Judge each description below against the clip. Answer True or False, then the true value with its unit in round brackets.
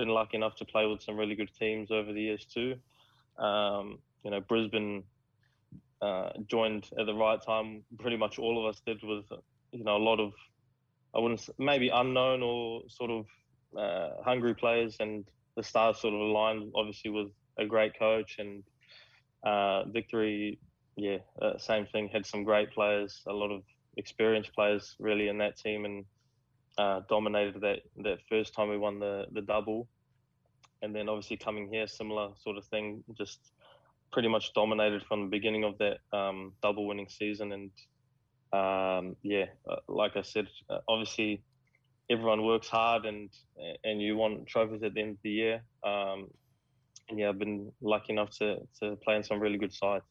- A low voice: True (110 Hz)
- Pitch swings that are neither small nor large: False (1.7 semitones)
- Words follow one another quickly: False (175 wpm)